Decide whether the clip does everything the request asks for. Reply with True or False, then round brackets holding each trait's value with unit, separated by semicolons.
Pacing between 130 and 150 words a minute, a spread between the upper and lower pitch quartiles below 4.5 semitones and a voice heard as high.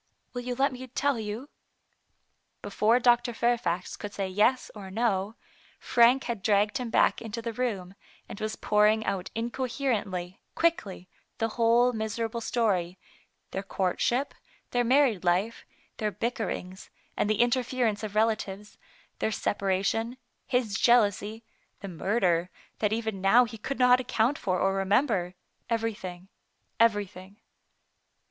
True (140 wpm; 3.5 semitones; 220 Hz)